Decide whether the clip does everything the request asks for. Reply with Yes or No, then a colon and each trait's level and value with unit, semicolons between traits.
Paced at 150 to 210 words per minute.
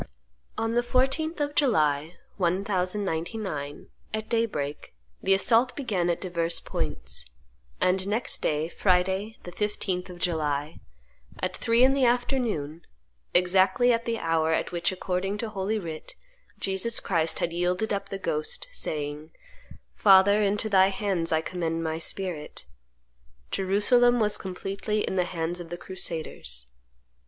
No: slow, 135 wpm